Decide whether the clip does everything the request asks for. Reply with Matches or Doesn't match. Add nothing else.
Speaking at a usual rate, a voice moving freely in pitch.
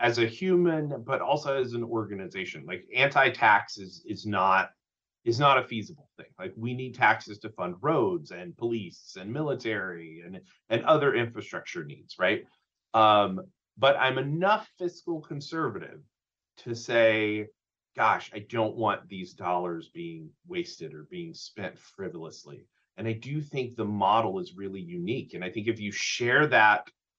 Matches